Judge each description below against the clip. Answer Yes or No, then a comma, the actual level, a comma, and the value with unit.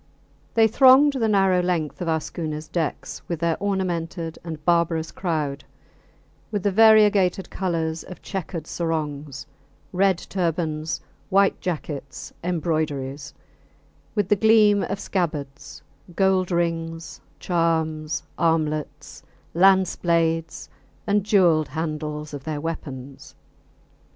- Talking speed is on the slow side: Yes, slow, 110 wpm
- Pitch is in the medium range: Yes, medium, 165 Hz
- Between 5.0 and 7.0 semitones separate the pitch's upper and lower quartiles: No, average, 3.5 semitones